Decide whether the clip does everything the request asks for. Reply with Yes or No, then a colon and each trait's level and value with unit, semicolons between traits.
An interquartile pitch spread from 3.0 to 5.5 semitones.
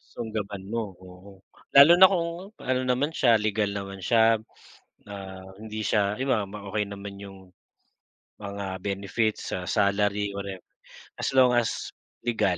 No: narrow, 2.6 semitones